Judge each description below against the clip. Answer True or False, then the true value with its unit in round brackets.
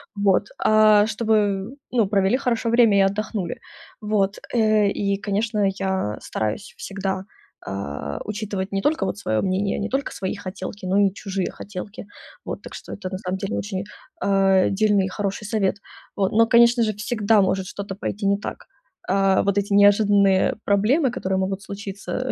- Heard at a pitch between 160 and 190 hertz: False (200 Hz)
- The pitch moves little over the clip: True (1.9 semitones)